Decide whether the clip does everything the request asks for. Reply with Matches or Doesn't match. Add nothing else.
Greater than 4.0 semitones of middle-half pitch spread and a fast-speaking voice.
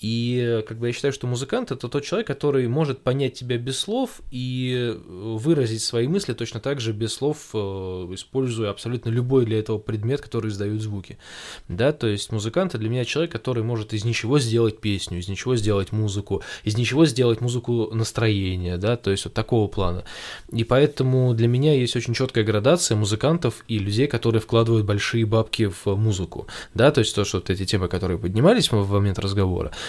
Doesn't match